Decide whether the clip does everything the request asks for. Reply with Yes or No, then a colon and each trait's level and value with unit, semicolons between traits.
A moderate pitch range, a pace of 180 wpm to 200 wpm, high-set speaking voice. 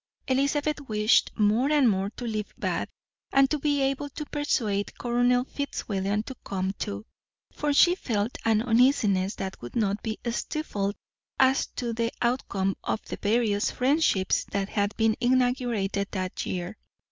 No: average, 4.7 semitones; average, 150 wpm; high, 225 Hz